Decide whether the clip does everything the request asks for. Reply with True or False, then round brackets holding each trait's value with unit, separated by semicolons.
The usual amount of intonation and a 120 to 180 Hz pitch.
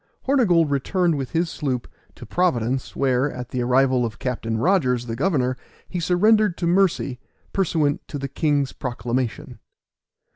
False (5.7 semitones; 140 Hz)